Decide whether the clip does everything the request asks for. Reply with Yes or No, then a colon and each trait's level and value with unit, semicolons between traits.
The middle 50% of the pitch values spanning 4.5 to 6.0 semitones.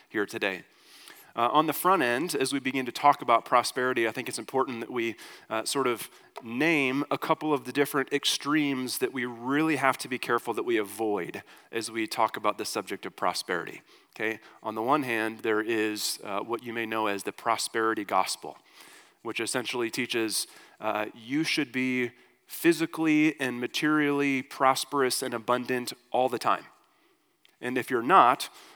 No: average, 3.5 semitones